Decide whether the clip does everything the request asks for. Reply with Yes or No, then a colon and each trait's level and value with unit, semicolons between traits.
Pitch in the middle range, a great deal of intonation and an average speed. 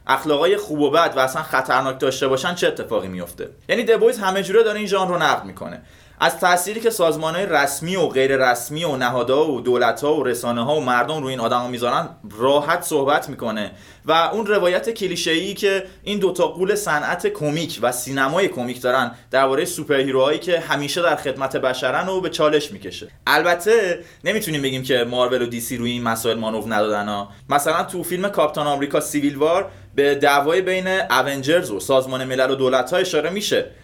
No: medium, 150 Hz; wide, 6.0 semitones; fast, 185 wpm